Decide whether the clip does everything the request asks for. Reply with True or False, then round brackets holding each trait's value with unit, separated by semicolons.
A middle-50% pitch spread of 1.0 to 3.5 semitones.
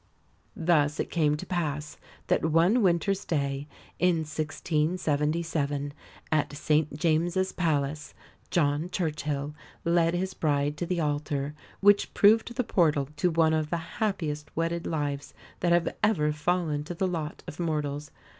True (2.8 semitones)